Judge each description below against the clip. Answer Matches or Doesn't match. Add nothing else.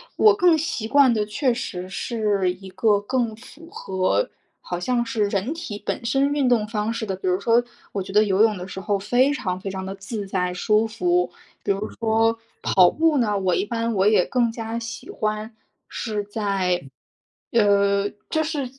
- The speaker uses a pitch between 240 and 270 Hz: Doesn't match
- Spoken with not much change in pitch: Doesn't match